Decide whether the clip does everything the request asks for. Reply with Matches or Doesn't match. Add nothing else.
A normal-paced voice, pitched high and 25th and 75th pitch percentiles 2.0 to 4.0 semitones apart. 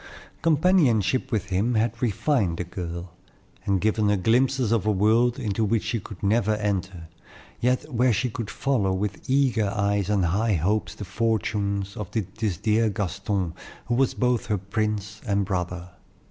Doesn't match